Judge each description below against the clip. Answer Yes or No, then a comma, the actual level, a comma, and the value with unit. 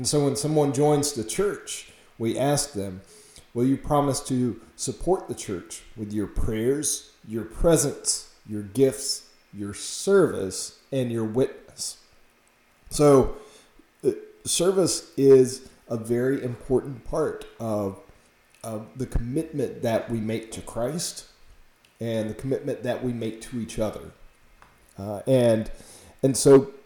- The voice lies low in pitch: Yes, low, 130 Hz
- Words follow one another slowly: Yes, slow, 130 wpm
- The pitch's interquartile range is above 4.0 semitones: Yes, average, 4.4 semitones